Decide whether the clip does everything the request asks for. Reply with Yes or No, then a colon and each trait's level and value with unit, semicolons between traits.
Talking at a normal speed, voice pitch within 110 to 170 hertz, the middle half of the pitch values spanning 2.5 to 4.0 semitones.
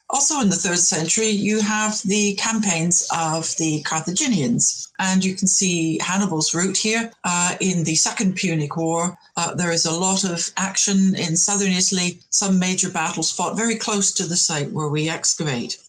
No: average, 180 wpm; medium, 185 Hz; average, 3.4 semitones